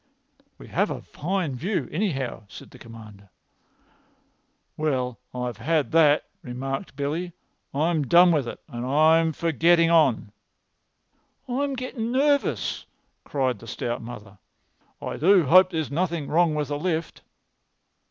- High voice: No, medium, 155 Hz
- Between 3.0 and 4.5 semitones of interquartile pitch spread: No, average, 5.3 semitones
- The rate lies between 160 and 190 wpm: No, slow, 135 wpm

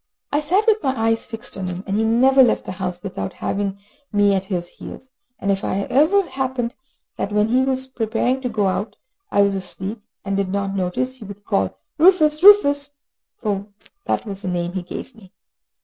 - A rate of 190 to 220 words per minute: Yes, average, 200 wpm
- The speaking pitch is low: No, high, 215 Hz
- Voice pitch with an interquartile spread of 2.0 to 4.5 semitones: No, average, 5.2 semitones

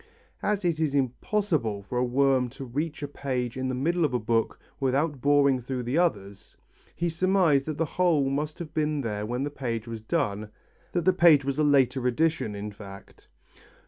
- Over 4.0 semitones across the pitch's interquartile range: Yes, average, 4.4 semitones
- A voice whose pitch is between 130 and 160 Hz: Yes, low, 135 Hz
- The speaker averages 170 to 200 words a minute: Yes, average, 195 wpm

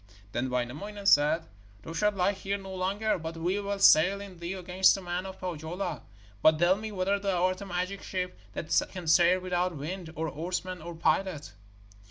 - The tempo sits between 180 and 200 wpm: Yes, average, 190 wpm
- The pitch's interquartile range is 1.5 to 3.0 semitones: Yes, average, 2.7 semitones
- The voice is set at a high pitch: No, medium, 180 Hz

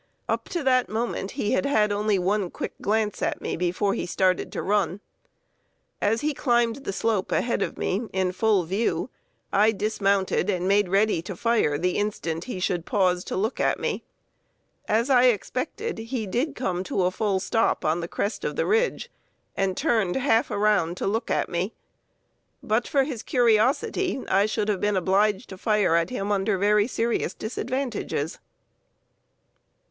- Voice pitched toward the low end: No, high, 210 Hz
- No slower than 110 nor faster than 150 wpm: No, average, 175 wpm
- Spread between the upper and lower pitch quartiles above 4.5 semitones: No, average, 3.7 semitones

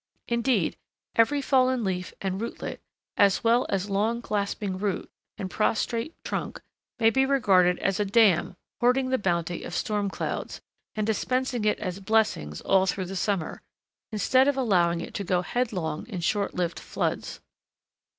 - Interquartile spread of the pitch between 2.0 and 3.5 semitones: No, average, 4.2 semitones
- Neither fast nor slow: Yes, average, 155 wpm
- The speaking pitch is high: Yes, high, 205 Hz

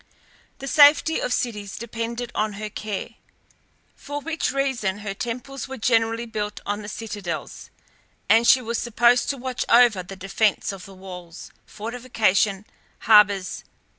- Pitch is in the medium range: No, high, 225 Hz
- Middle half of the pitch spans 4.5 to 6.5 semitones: No, average, 3.3 semitones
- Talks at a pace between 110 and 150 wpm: Yes, average, 145 wpm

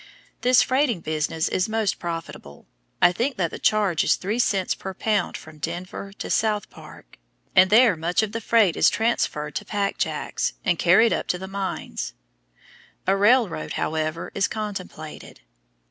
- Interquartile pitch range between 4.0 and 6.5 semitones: Yes, average, 4.6 semitones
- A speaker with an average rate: Yes, average, 160 wpm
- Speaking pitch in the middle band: No, high, 195 Hz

